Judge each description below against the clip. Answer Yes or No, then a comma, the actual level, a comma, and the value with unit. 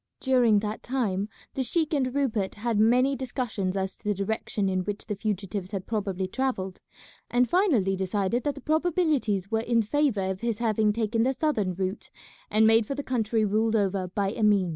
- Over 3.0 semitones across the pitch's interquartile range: Yes, average, 4.2 semitones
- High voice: Yes, high, 220 Hz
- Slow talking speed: No, average, 185 wpm